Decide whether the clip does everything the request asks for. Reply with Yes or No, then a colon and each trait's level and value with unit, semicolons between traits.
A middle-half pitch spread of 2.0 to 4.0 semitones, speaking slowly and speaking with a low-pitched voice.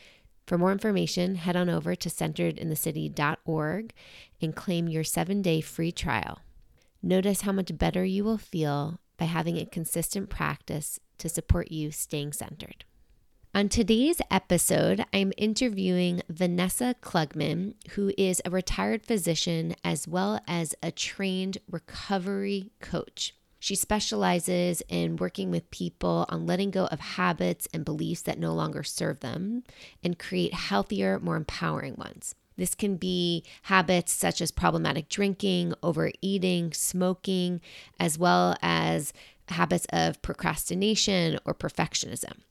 No: average, 3.5 semitones; slow, 130 wpm; medium, 175 Hz